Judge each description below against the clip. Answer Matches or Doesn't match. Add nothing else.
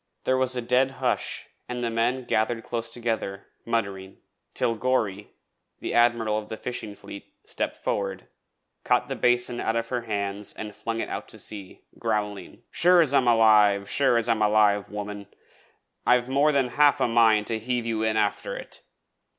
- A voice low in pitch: Matches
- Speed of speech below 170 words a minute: Doesn't match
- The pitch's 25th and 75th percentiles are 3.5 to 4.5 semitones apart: Doesn't match